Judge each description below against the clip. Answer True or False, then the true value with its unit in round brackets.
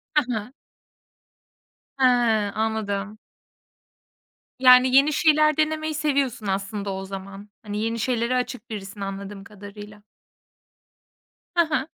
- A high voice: True (220 Hz)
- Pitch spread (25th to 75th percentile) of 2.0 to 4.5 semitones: False (4.9 semitones)